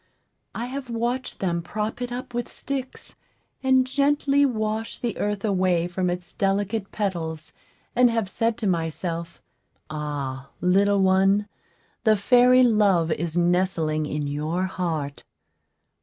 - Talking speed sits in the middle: No, slow, 130 wpm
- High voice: Yes, high, 195 Hz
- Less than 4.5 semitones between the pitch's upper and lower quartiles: No, wide, 5.5 semitones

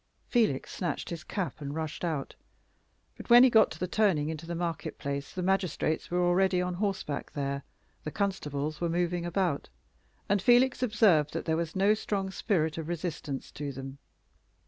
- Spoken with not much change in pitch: No, average, 4.2 semitones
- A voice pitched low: No, medium, 175 Hz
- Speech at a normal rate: Yes, average, 175 wpm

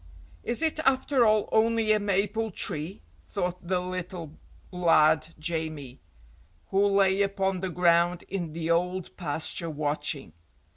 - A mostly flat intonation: No, average, 3.6 semitones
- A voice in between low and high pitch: Yes, medium, 180 Hz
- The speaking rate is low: Yes, slow, 130 wpm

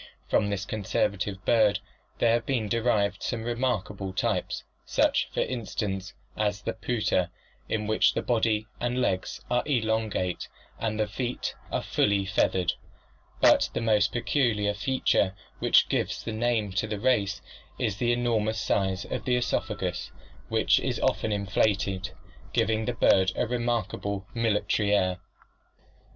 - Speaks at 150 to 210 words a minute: No, average, 140 wpm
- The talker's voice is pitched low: Yes, low, 105 Hz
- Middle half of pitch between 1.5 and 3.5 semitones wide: Yes, average, 2.8 semitones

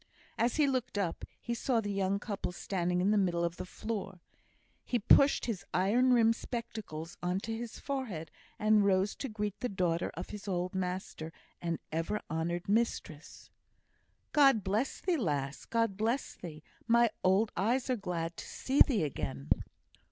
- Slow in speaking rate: No, average, 165 wpm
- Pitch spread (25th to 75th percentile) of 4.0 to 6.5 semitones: Yes, average, 4.7 semitones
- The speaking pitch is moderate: No, high, 200 Hz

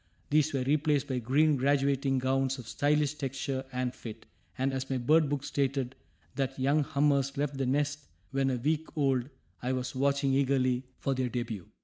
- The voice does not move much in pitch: Yes, narrow, 1.7 semitones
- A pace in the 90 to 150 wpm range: No, average, 175 wpm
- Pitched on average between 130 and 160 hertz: Yes, low, 135 Hz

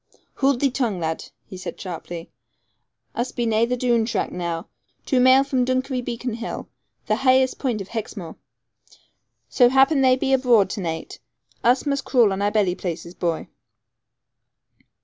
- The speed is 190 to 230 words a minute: No, average, 160 wpm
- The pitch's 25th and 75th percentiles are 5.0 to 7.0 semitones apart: Yes, average, 5.3 semitones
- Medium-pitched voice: No, high, 235 Hz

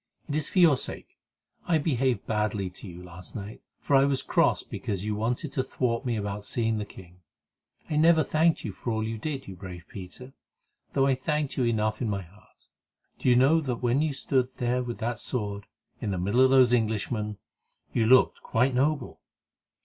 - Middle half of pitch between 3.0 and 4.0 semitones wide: No, average, 4.4 semitones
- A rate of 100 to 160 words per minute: No, average, 200 wpm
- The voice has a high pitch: No, low, 120 Hz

